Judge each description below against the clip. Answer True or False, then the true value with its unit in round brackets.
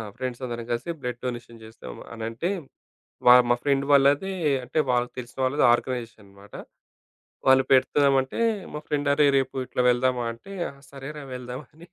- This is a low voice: True (130 Hz)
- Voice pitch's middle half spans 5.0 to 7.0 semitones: False (2.7 semitones)